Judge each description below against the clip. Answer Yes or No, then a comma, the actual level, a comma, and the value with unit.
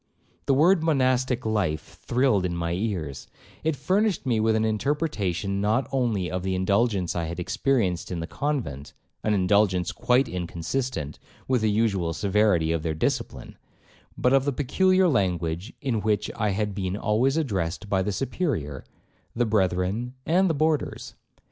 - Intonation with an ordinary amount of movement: No, wide, 6.3 semitones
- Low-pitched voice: Yes, low, 105 Hz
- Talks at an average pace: Yes, average, 155 wpm